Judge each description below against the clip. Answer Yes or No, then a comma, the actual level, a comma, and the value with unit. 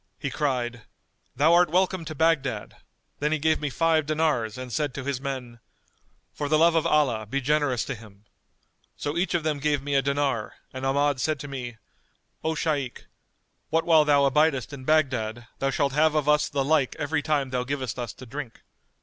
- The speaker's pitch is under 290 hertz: Yes, medium, 140 Hz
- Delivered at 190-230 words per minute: Yes, average, 195 wpm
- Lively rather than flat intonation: No, average, 3.2 semitones